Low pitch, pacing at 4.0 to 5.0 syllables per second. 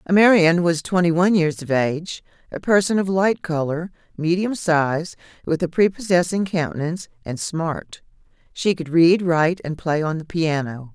No: medium, 170 Hz; 4.8 syllables/s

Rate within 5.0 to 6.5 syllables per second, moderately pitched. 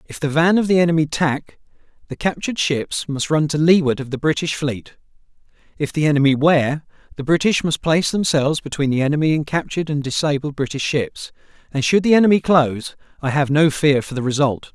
Yes: 5.8 syllables/s; medium, 150 Hz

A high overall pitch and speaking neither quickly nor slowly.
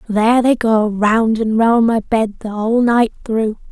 Yes: high, 225 Hz; average, 195 wpm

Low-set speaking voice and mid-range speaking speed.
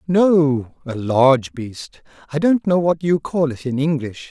No: medium, 145 Hz; average, 180 wpm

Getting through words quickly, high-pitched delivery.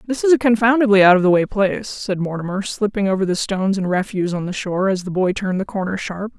Yes: fast, 255 wpm; high, 195 Hz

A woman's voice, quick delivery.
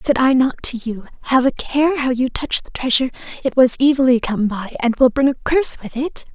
Yes: female; fast, 235 wpm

